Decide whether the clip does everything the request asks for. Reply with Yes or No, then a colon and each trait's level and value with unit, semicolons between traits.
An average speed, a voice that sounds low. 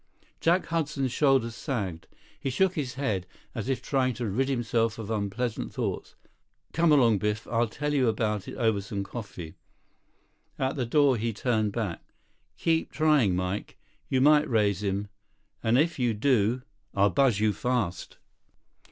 Yes: average, 155 wpm; low, 120 Hz